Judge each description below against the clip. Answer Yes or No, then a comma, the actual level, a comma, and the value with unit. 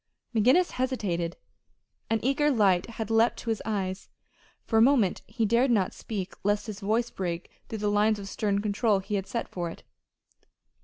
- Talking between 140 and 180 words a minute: Yes, average, 175 wpm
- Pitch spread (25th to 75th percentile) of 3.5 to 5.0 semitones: No, average, 2.9 semitones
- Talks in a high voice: Yes, high, 215 Hz